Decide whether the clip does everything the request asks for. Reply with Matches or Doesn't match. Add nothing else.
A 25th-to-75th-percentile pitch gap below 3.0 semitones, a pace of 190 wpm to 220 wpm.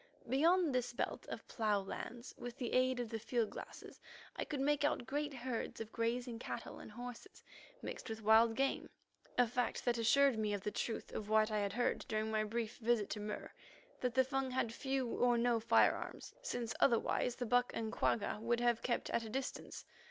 Matches